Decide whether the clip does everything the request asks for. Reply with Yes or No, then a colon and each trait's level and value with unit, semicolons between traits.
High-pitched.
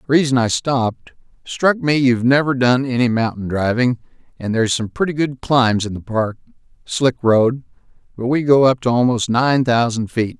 No: low, 125 Hz